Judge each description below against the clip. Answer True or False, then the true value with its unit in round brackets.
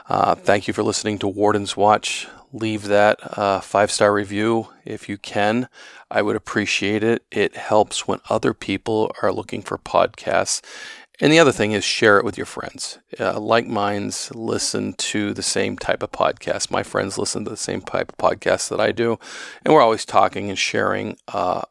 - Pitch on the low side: True (105 Hz)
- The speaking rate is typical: True (190 wpm)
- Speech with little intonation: True (1.4 semitones)